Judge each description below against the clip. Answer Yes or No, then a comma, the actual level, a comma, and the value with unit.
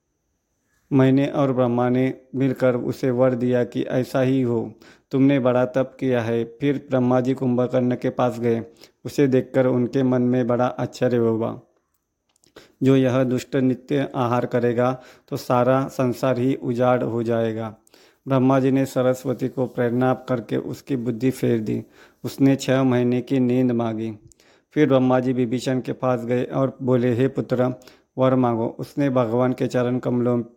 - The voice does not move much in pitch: Yes, narrow, 1.2 semitones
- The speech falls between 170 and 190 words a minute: No, average, 155 wpm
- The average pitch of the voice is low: Yes, low, 125 Hz